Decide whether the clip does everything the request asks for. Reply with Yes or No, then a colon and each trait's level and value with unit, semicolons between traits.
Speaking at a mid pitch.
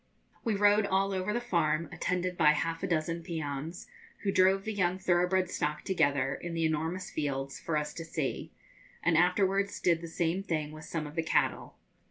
Yes: medium, 170 Hz